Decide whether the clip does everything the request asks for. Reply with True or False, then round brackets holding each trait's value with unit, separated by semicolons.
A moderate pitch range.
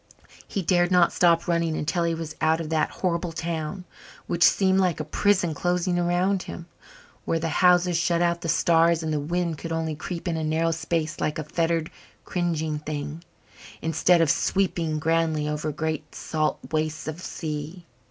False (1.9 semitones)